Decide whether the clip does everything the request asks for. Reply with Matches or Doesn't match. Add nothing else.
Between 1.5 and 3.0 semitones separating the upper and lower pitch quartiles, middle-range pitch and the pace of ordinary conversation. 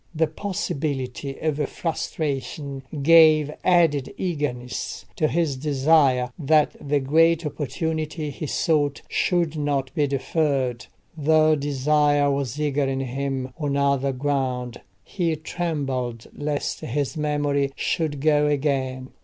Doesn't match